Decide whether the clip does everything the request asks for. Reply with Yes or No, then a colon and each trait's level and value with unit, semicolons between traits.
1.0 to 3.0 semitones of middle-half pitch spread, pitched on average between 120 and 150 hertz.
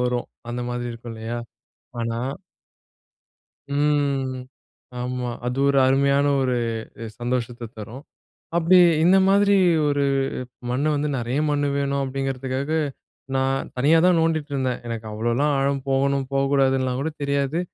Yes: narrow, 2.4 semitones; low, 135 Hz